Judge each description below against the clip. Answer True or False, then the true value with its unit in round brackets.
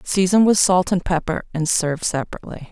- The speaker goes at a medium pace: True (175 wpm)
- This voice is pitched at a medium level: True (175 Hz)